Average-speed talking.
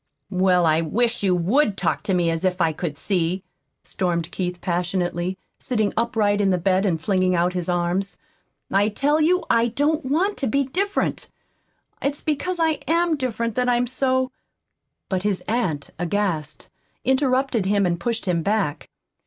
Yes: average, 170 wpm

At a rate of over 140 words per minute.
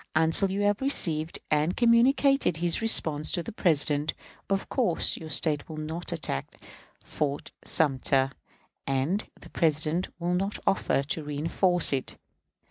No: slow, 135 wpm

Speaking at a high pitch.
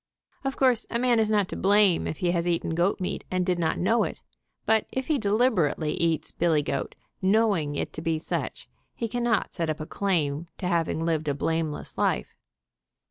No: medium, 175 Hz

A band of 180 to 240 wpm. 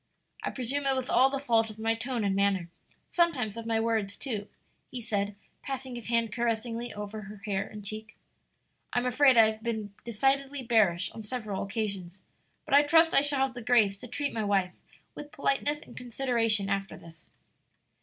Yes: average, 185 wpm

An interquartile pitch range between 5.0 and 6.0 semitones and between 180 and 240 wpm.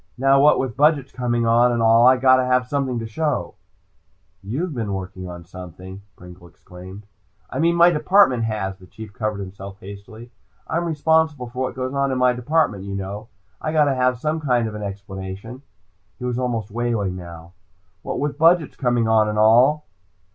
Yes: wide, 5.4 semitones; average, 185 wpm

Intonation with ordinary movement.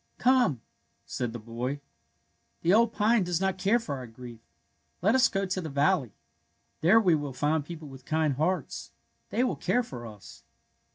No: wide, 7.2 semitones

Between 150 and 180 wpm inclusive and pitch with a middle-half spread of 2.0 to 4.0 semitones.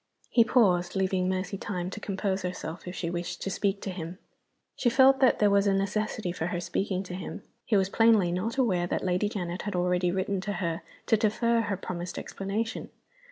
No: fast, 205 wpm; average, 2.8 semitones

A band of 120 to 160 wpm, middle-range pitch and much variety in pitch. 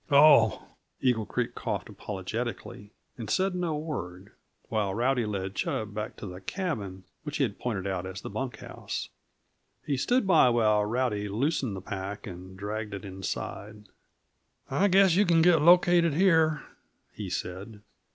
No: average, 155 wpm; low, 110 Hz; wide, 7.7 semitones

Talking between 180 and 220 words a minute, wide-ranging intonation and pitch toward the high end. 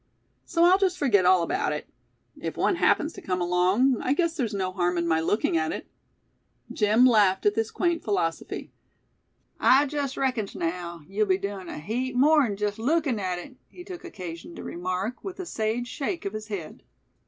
Yes: average, 190 wpm; wide, 6.9 semitones; high, 215 Hz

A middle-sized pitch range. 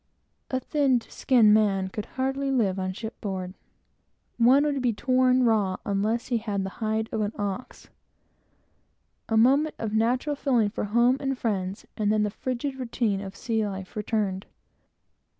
Yes: average, 3.8 semitones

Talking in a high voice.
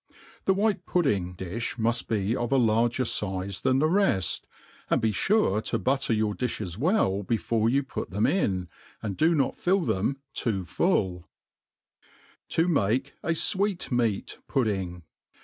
No: low, 115 Hz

